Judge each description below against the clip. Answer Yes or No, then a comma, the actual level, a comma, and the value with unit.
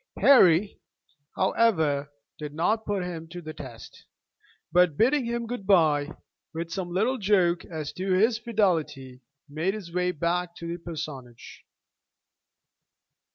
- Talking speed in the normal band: No, slow, 130 wpm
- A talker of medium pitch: Yes, medium, 175 Hz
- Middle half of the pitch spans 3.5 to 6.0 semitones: Yes, average, 4.5 semitones